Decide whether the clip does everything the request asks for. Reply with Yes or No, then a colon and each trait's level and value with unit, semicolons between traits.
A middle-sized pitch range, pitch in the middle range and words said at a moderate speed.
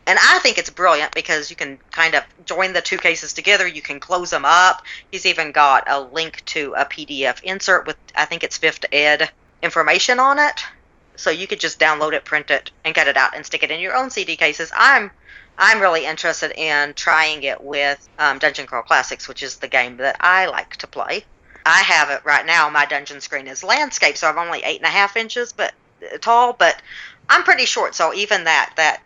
No: average, 4.1 semitones; medium, 165 Hz; fast, 220 wpm